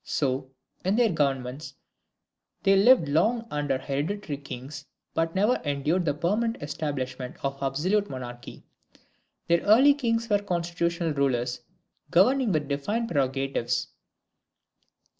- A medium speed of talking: No, slow, 115 wpm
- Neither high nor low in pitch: Yes, medium, 155 Hz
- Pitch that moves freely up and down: Yes, wide, 6.9 semitones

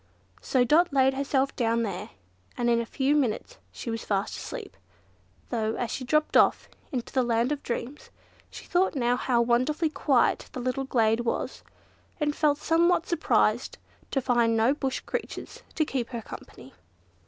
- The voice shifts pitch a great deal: No, average, 3.9 semitones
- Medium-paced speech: Yes, average, 165 wpm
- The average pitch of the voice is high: Yes, very high, 255 Hz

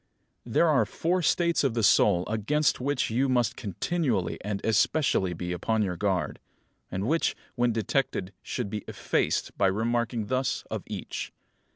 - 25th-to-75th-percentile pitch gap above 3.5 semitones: Yes, average, 5.3 semitones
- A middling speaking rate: Yes, average, 160 wpm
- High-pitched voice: No, low, 115 Hz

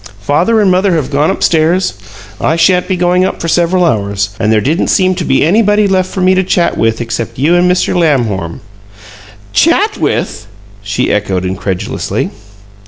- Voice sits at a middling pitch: Yes, medium, 165 Hz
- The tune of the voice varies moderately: No, wide, 8.6 semitones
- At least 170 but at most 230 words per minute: Yes, average, 175 wpm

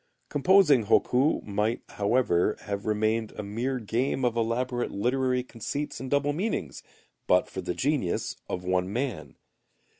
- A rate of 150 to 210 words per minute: No, average, 140 wpm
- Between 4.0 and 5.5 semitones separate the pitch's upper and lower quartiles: Yes, average, 4.4 semitones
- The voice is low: Yes, low, 115 Hz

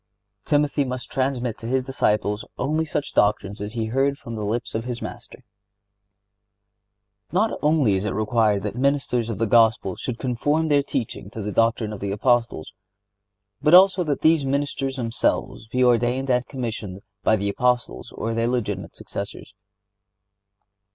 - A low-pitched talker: Yes, low, 120 Hz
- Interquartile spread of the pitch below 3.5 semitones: No, average, 4.0 semitones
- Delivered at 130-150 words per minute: No, average, 160 wpm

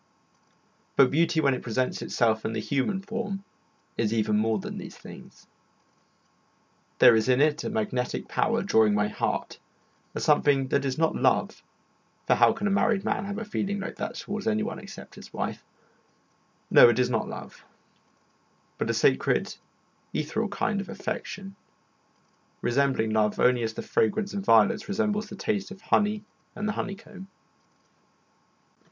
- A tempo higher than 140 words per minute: Yes, average, 160 wpm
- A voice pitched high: No, medium, 165 Hz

